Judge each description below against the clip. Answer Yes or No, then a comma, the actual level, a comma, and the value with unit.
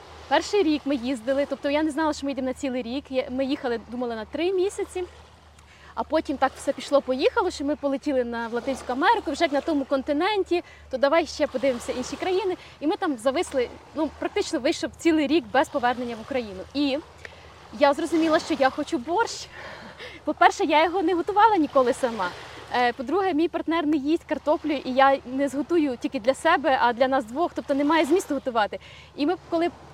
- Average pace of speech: No, fast, 185 wpm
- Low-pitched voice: No, very high, 290 Hz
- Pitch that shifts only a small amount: No, average, 3.8 semitones